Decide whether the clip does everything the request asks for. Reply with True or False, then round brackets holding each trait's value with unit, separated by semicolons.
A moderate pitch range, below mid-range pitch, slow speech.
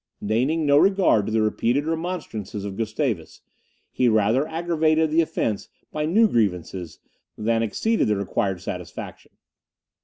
False (7.3 semitones; 120 Hz; 130 wpm)